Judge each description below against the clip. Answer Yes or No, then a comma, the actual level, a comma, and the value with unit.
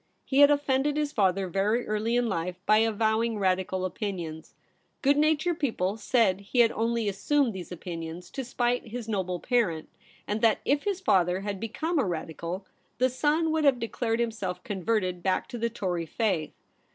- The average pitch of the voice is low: No, high, 220 Hz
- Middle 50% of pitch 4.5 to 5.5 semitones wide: Yes, average, 5.1 semitones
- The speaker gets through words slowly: No, average, 175 wpm